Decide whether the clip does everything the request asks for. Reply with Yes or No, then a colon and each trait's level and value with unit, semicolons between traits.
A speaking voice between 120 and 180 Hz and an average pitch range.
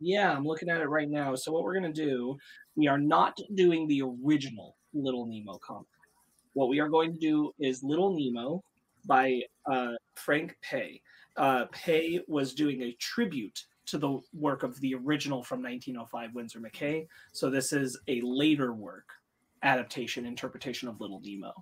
Yes: medium, 140 Hz; average, 4.1 semitones